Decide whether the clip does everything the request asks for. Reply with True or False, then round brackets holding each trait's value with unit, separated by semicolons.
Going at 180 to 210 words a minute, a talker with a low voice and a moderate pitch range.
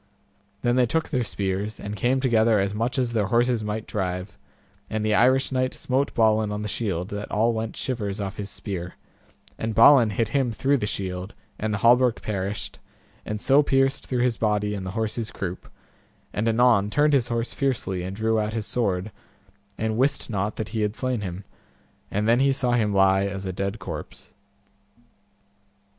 True (185 wpm; 110 Hz; 3.3 semitones)